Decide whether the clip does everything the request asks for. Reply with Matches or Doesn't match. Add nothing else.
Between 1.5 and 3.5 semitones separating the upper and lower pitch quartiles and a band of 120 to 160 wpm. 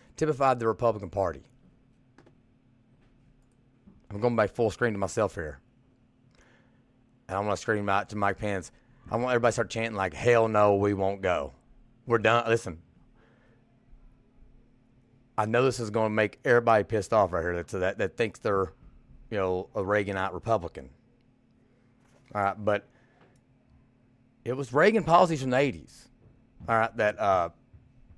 Matches